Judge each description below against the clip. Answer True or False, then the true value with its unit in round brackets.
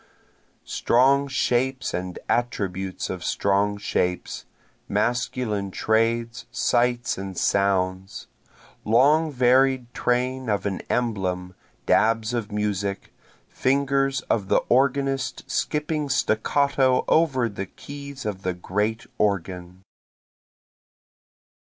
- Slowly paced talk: True (95 wpm)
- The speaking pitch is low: True (115 Hz)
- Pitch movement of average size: True (5.0 semitones)